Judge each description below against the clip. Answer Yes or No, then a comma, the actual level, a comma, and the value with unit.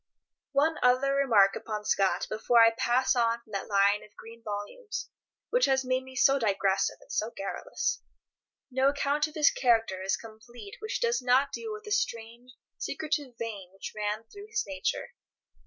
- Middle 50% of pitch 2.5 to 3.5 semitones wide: No, average, 4.7 semitones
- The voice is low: No, high, 240 Hz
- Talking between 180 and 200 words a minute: No, average, 170 wpm